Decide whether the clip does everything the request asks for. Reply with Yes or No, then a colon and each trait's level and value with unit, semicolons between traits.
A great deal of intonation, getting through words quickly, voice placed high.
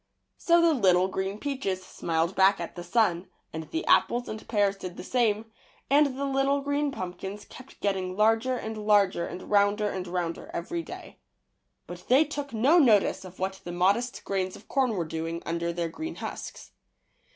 No: wide, 5.9 semitones; average, 185 wpm; high, 205 Hz